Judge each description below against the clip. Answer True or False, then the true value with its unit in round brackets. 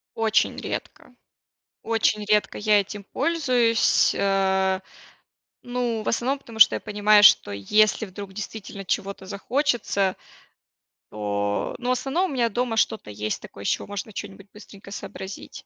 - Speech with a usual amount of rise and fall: True (3.0 semitones)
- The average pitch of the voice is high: True (210 Hz)